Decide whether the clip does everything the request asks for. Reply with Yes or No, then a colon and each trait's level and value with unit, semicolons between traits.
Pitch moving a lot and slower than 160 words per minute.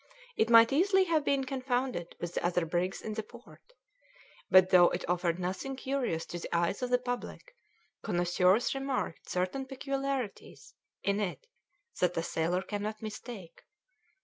Yes: wide, 6.7 semitones; average, 150 wpm